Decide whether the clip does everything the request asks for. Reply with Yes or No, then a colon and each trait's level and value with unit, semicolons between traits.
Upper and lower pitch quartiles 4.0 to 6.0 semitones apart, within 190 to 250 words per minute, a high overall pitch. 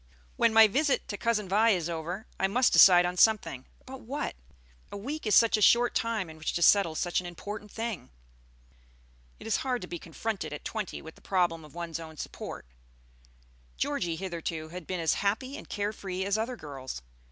Yes: average, 5.0 semitones; average, 200 wpm; high, 195 Hz